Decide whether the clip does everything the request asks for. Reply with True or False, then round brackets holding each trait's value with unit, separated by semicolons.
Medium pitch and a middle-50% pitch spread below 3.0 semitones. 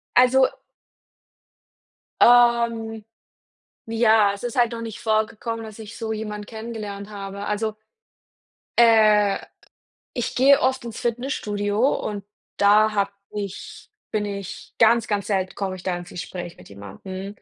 False (215 Hz; 2.4 semitones)